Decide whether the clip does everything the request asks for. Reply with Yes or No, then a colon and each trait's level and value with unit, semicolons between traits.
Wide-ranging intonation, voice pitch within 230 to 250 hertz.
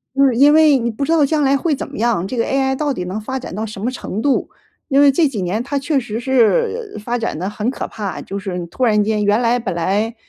No: average, 4.7 semitones; high, 240 Hz